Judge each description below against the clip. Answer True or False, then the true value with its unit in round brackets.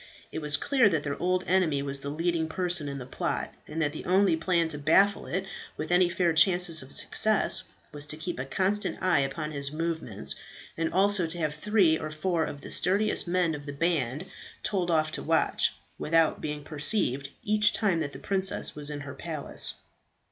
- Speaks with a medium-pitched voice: True (165 Hz)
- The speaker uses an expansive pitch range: False (3.7 semitones)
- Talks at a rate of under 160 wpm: False (200 wpm)